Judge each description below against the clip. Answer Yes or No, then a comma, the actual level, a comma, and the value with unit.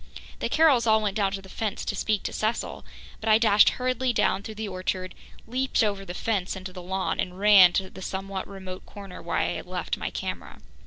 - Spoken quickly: Yes, fast, 220 wpm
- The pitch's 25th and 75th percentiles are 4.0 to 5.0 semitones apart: No, narrow, 2.5 semitones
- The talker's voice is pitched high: Yes, high, 200 Hz